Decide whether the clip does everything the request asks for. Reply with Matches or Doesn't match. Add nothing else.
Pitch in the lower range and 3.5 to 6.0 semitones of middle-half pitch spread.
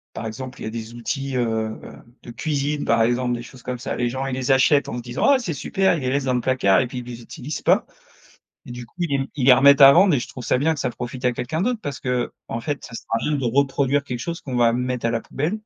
Doesn't match